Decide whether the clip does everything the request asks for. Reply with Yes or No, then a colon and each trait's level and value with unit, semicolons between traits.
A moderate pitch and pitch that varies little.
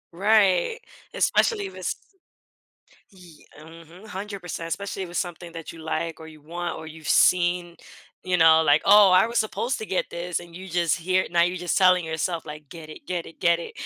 Yes: medium, 175 Hz; narrow, 2.3 semitones